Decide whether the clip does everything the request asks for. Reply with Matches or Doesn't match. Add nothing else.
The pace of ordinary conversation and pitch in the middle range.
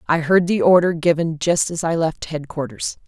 Matches